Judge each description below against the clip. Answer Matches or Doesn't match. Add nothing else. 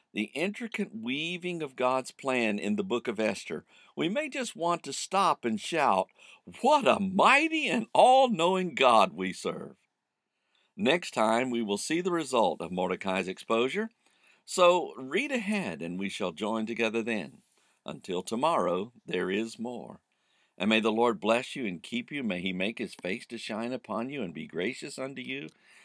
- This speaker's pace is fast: Doesn't match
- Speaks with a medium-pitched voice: Doesn't match